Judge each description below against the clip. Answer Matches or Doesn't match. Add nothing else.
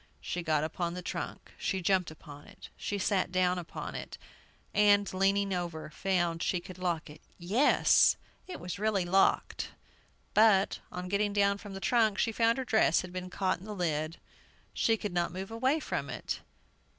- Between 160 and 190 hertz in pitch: Matches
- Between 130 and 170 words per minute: Doesn't match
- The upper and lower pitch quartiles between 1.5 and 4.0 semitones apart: Matches